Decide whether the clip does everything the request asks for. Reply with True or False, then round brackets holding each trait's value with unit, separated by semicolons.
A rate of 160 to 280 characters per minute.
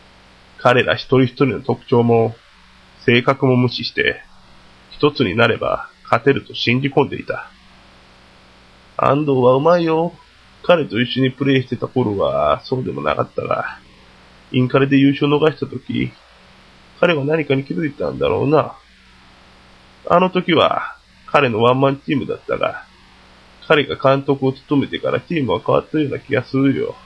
False (290 characters per minute)